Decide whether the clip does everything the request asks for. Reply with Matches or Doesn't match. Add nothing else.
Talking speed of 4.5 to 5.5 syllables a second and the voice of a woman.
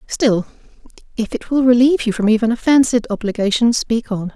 Doesn't match